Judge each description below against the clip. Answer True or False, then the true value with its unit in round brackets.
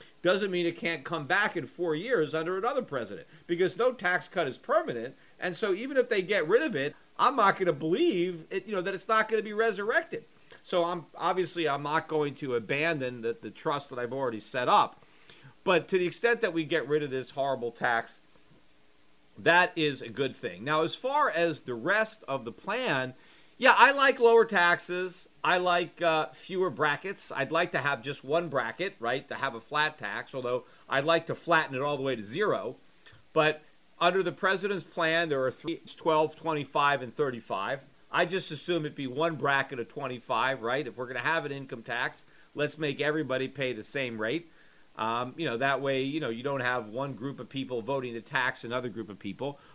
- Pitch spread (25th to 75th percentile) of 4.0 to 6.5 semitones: True (5.2 semitones)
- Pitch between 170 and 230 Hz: False (155 Hz)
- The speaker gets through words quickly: True (210 wpm)